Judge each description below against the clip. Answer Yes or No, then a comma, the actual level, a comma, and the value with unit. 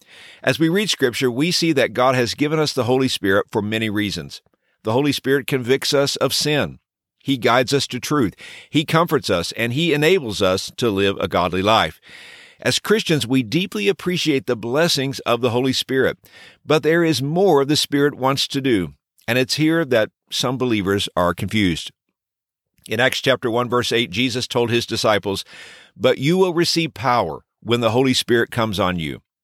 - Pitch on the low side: Yes, low, 130 Hz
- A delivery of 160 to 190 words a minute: Yes, average, 185 wpm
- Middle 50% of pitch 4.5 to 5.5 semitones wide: Yes, average, 5.1 semitones